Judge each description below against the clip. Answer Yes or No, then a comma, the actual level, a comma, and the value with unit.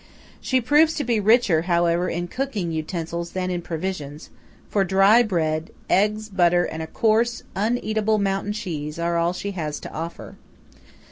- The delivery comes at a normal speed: Yes, average, 155 wpm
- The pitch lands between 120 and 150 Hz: No, medium, 185 Hz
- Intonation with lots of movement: No, average, 4.2 semitones